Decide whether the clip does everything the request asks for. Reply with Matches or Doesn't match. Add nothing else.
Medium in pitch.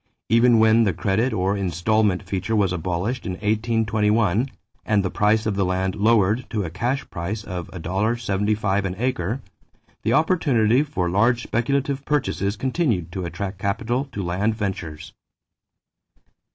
Doesn't match